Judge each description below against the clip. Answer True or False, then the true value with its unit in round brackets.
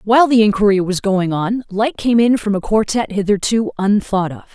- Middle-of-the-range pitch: False (210 Hz)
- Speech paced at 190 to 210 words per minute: True (200 wpm)